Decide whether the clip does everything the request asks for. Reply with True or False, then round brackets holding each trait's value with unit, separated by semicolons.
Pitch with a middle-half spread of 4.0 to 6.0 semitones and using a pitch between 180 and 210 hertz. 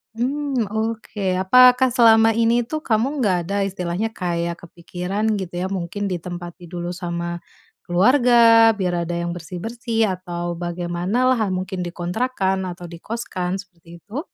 True (4.6 semitones; 190 Hz)